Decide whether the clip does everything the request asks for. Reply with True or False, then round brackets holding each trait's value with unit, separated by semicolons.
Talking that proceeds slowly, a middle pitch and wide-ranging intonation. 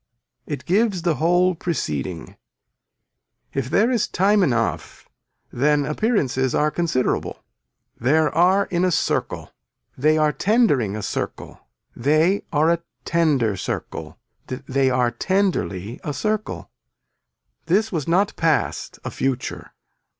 True (120 wpm; 155 Hz; 5.9 semitones)